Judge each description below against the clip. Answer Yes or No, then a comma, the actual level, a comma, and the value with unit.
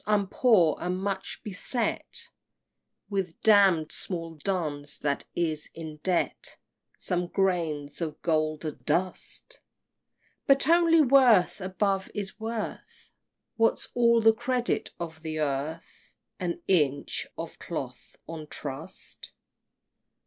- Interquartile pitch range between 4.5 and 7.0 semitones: Yes, average, 5.0 semitones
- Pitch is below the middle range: No, medium, 180 Hz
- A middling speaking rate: No, slow, 110 wpm